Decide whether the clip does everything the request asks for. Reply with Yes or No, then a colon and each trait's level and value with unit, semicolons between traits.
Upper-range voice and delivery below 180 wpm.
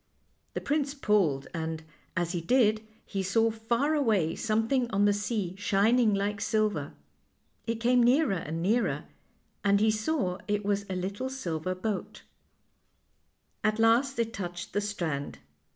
Yes: high, 210 Hz; average, 145 wpm